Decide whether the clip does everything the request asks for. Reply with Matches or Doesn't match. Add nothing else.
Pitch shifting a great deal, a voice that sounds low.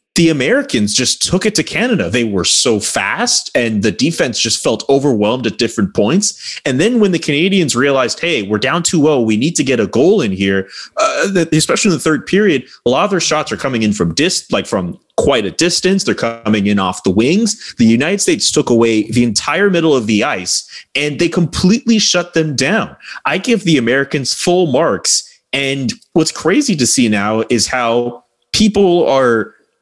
Doesn't match